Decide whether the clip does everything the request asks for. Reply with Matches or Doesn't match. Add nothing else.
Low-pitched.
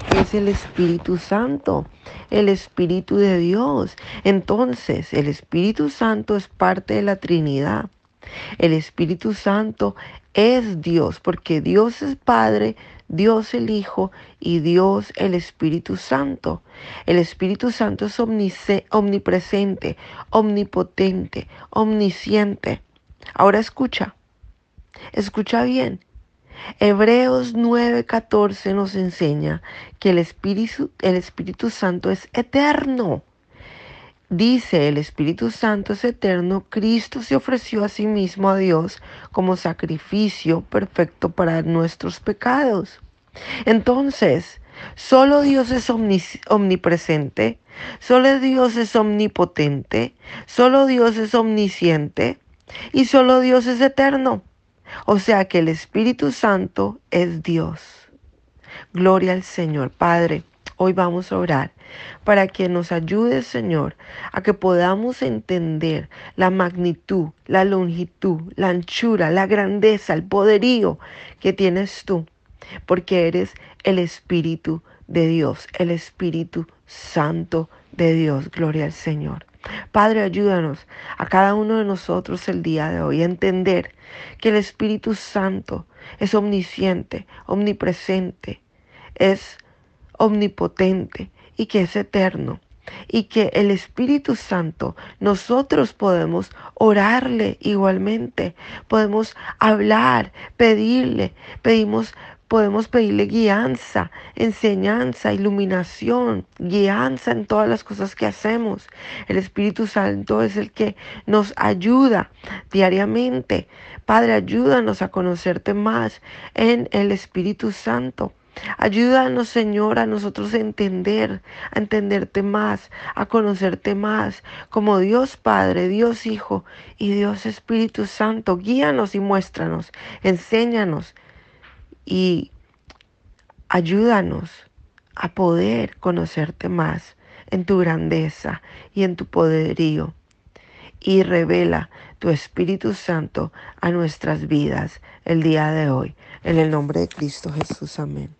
Doesn't match